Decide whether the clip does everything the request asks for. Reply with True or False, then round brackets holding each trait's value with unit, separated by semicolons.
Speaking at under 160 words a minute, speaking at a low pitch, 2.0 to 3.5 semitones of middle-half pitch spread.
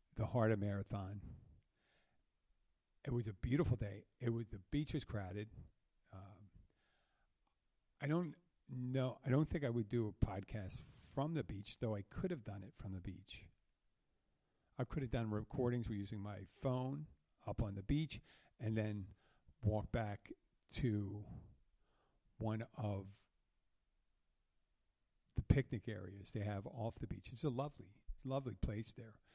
False (145 wpm; 110 Hz; 4.2 semitones)